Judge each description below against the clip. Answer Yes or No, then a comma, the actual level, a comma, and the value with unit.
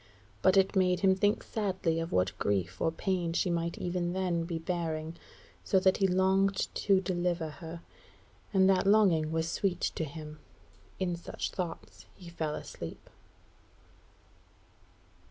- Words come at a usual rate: Yes, average, 145 wpm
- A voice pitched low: No, medium, 175 Hz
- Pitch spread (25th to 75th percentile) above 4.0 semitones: No, narrow, 2.6 semitones